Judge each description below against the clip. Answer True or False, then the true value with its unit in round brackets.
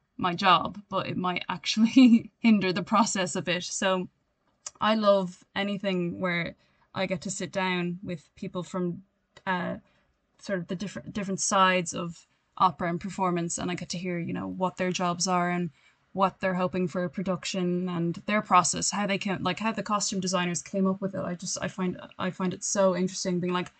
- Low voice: False (185 Hz)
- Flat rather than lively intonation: True (1.6 semitones)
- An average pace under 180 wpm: False (200 wpm)